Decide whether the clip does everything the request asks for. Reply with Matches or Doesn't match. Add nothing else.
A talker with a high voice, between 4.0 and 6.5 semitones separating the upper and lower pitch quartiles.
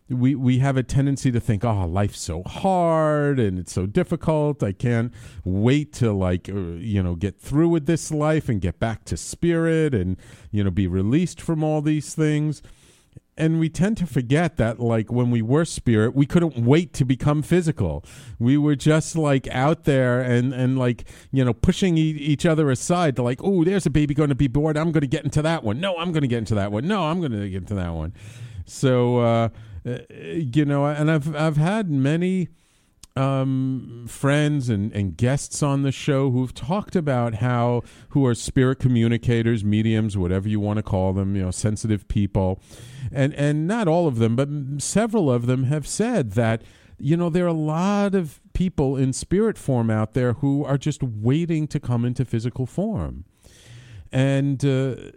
Doesn't match